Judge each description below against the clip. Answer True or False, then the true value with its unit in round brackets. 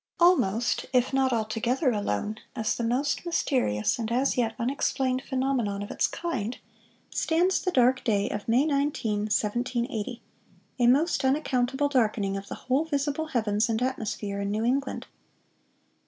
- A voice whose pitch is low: False (245 Hz)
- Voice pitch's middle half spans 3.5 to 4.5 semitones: True (4.1 semitones)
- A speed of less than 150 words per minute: True (140 wpm)